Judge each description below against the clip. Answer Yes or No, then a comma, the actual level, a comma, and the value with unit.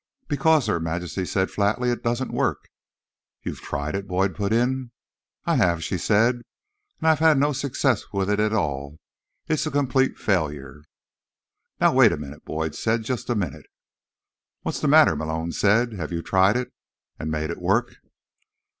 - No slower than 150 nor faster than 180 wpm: Yes, average, 170 wpm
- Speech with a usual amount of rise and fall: No, wide, 7.1 semitones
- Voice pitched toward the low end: Yes, low, 100 Hz